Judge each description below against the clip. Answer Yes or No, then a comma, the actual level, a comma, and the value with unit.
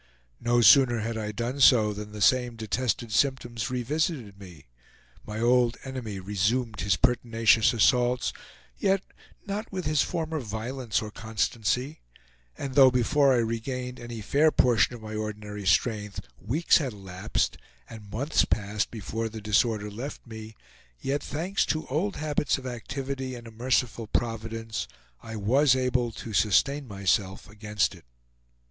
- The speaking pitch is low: Yes, low, 115 Hz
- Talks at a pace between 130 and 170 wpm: Yes, average, 145 wpm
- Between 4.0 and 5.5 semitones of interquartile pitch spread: No, average, 3.5 semitones